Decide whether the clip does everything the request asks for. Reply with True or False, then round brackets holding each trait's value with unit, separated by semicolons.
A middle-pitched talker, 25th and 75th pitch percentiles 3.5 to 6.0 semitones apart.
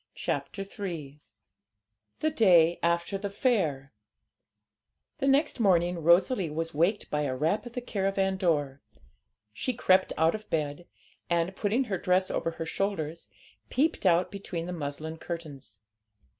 True (175 Hz; 3.8 semitones)